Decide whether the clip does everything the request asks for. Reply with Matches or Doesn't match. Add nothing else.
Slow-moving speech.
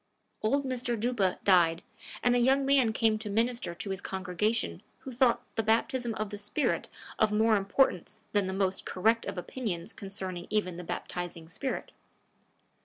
Doesn't match